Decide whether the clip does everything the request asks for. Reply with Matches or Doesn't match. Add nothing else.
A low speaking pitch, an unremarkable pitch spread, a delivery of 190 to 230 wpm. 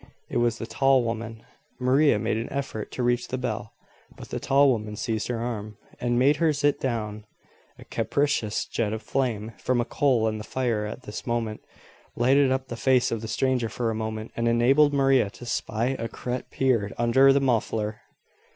Matches